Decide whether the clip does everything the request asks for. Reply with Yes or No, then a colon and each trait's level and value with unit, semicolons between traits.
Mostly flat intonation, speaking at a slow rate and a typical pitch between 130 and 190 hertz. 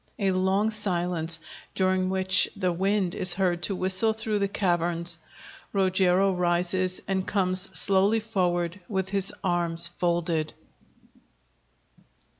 Yes: narrow, 1.9 semitones; slow, 115 wpm; medium, 185 Hz